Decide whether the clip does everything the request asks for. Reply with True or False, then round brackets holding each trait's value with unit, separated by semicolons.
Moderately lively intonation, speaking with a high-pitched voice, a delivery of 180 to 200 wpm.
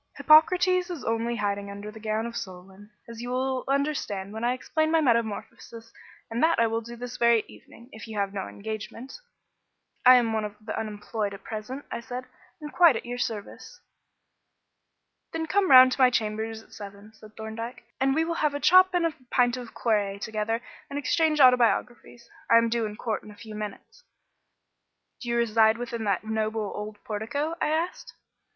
True (3.4 semitones; 230 Hz; 190 wpm)